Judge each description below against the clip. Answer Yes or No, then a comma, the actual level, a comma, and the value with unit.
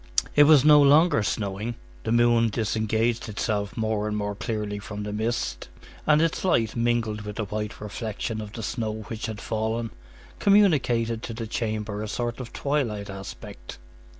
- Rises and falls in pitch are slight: Yes, narrow, 2.1 semitones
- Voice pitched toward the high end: No, low, 110 Hz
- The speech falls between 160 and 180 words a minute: Yes, average, 165 wpm